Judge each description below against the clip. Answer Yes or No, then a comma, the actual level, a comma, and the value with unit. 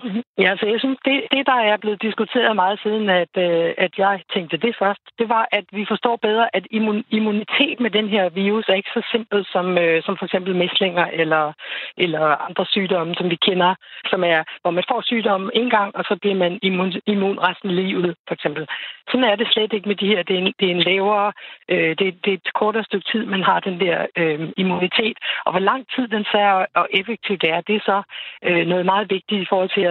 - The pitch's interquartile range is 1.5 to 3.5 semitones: Yes, average, 3.1 semitones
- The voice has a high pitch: Yes, high, 195 Hz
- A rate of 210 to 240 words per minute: Yes, average, 220 wpm